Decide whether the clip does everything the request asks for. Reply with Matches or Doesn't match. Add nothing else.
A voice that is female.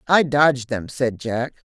Matches